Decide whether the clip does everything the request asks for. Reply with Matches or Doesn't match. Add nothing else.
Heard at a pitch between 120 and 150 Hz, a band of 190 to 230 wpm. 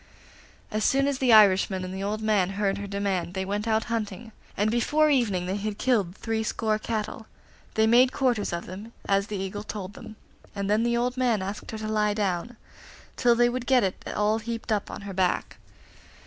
Doesn't match